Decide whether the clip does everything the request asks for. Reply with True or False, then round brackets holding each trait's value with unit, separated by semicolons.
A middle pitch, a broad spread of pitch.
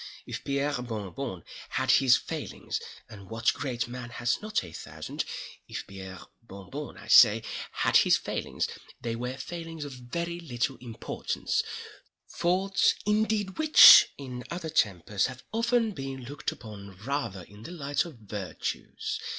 False (130 Hz; 6.6 semitones)